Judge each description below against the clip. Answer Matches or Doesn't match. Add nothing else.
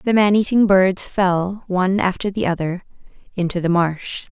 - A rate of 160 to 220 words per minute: Doesn't match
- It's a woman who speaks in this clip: Matches